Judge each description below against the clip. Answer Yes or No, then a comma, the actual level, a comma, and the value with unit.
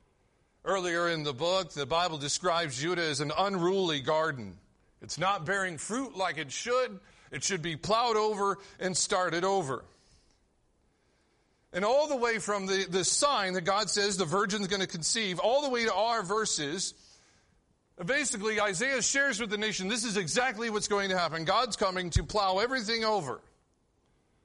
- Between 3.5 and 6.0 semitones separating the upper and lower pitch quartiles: Yes, average, 3.9 semitones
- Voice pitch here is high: Yes, high, 195 Hz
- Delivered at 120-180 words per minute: Yes, average, 165 wpm